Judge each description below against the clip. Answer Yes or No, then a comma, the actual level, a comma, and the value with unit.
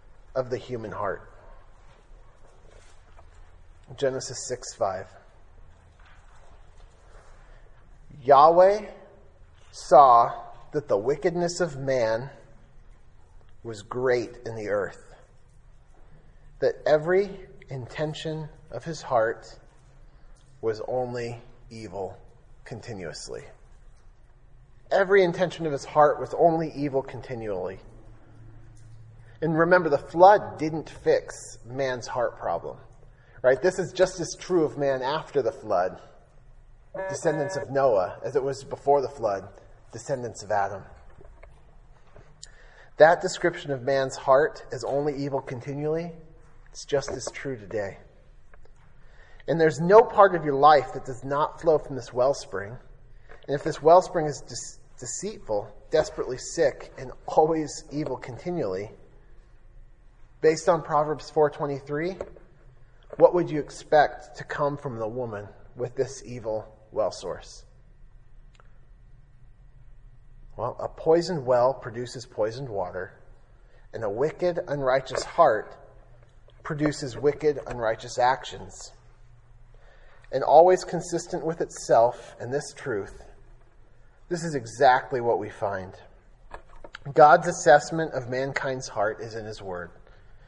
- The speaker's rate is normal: No, slow, 110 wpm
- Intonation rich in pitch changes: No, average, 4.9 semitones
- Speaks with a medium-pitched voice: No, low, 130 Hz